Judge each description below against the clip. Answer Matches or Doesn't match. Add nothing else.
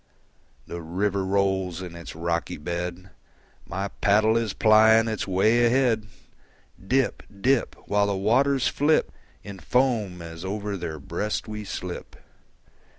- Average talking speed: Doesn't match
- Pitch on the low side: Matches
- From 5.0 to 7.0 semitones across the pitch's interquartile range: Doesn't match